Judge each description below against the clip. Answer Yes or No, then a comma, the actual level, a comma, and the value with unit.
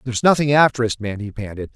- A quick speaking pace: Yes, fast, 240 wpm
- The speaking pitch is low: Yes, low, 120 Hz